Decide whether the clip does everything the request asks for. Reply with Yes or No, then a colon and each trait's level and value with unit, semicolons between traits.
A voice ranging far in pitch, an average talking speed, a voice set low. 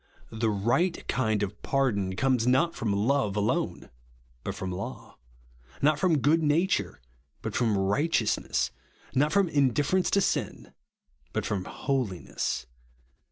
No: wide, 6.5 semitones; slow, 125 wpm; low, 130 Hz